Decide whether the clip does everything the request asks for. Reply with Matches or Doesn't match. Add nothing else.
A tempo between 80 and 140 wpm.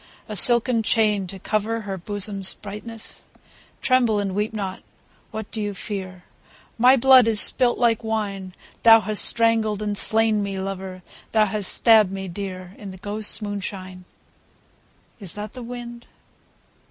Doesn't match